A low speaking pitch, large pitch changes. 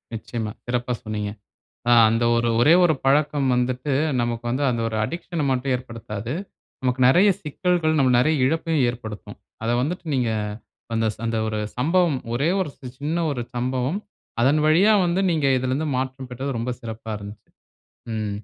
No: low, 130 Hz; average, 4.6 semitones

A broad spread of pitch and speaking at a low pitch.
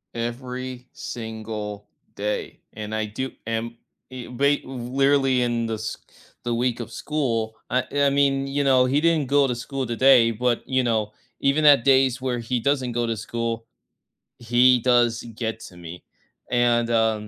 No: narrow, 2.5 semitones; low, 120 Hz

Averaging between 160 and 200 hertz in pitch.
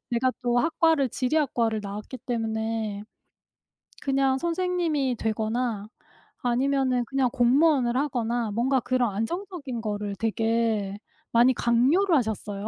No: high, 245 Hz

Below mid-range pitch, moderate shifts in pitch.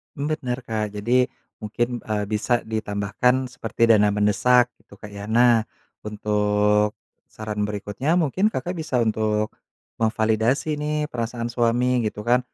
Yes: low, 115 Hz; average, 3.0 semitones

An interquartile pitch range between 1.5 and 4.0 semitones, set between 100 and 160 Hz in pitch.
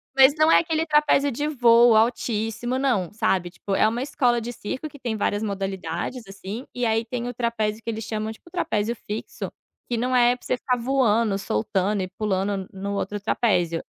No: average, 3.4 semitones; high, 225 Hz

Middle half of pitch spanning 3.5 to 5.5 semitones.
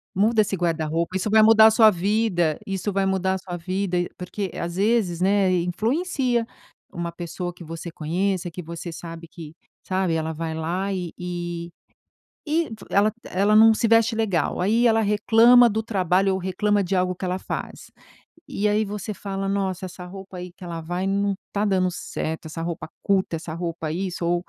No: average, 3.1 semitones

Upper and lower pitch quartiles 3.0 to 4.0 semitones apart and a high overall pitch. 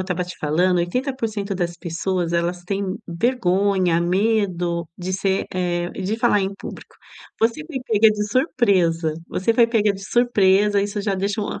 Yes: average, 3.3 semitones; high, 195 Hz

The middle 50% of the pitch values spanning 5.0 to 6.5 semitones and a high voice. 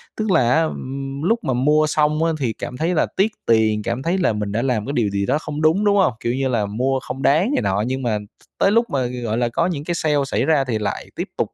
No: average, 5.3 semitones; low, 135 Hz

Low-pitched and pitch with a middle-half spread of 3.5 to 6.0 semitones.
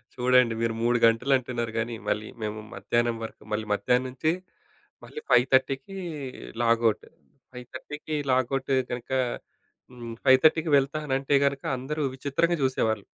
No: low, 125 Hz; average, 2.7 semitones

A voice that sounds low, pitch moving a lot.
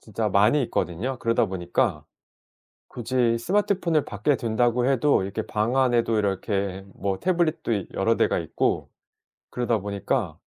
No: low, 115 Hz; average, 4.6 semitones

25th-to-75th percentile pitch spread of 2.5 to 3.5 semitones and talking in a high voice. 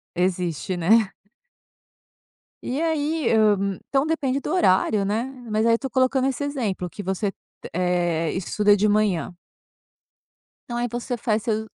No: wide, 5.5 semitones; high, 215 Hz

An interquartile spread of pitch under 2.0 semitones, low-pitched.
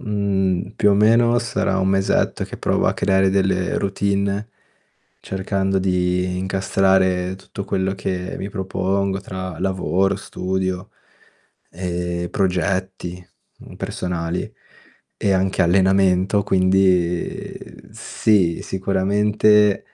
Yes: narrow, 1.2 semitones; very low, 95 Hz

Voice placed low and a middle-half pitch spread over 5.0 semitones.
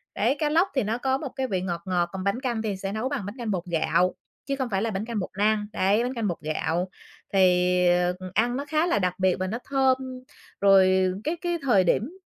No: high, 210 Hz; wide, 5.6 semitones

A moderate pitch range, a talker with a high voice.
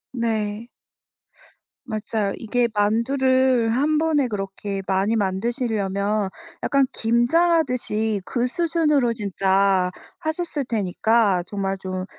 Yes: average, 4.6 semitones; high, 225 Hz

